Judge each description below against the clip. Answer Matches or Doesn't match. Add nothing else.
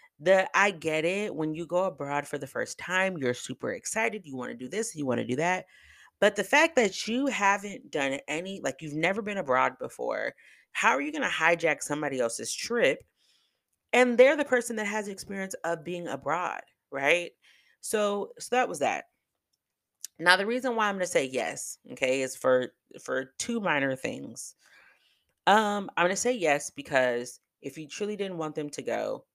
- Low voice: Doesn't match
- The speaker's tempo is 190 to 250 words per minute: Matches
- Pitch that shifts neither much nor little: Doesn't match